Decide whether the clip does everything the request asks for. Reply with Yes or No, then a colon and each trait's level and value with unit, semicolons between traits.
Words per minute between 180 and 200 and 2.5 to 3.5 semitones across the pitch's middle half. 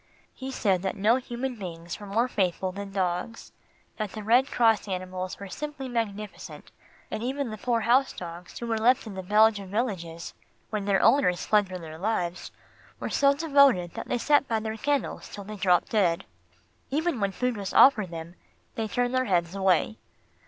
No: average, 185 wpm; average, 4.8 semitones